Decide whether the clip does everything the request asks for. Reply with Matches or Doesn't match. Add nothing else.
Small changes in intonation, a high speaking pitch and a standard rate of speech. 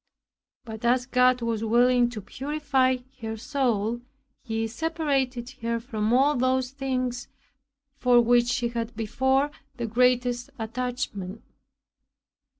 Doesn't match